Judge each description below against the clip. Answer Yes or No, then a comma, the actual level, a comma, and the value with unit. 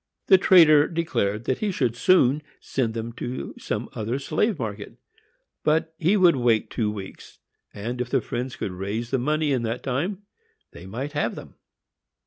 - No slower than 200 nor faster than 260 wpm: No, average, 165 wpm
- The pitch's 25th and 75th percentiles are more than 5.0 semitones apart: Yes, wide, 5.5 semitones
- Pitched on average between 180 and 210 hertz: No, low, 130 Hz